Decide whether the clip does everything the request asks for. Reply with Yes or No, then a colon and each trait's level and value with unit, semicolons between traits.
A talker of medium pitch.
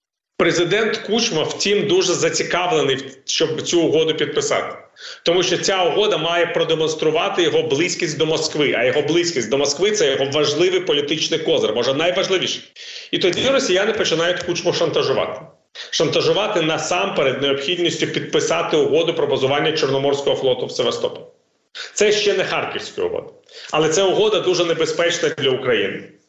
No: very high, 370 Hz